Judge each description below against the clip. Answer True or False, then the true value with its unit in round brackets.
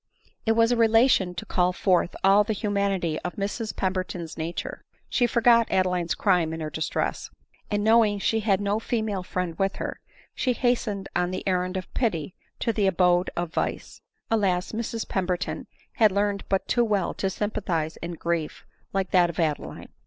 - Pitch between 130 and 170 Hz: False (195 Hz)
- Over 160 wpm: True (175 wpm)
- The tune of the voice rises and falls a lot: False (3.4 semitones)